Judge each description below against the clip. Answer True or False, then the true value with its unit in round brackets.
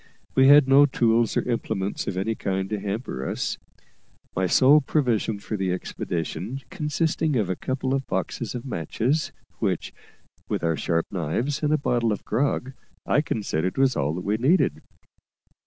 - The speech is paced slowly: False (165 wpm)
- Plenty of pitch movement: True (6.2 semitones)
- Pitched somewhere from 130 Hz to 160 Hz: False (115 Hz)